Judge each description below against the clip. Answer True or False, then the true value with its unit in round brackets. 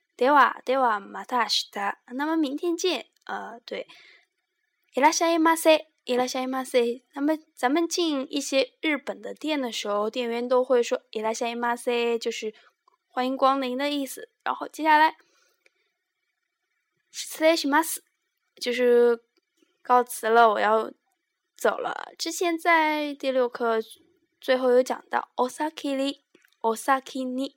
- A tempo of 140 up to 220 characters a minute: True (215 characters per minute)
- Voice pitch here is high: True (275 Hz)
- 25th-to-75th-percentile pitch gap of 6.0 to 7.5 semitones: False (5.1 semitones)